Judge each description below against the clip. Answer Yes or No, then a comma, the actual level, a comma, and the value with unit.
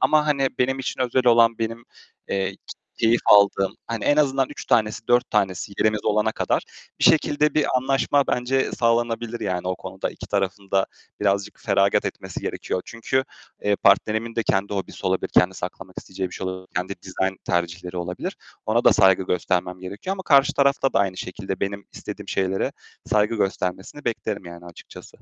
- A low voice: Yes, low, 105 Hz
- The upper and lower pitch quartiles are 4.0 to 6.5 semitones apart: Yes, average, 4.3 semitones